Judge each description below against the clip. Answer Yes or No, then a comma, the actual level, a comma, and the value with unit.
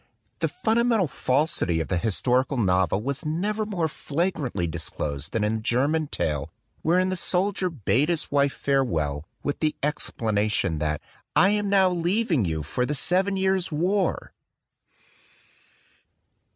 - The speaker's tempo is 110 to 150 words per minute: Yes, average, 145 wpm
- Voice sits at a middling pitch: Yes, medium, 145 Hz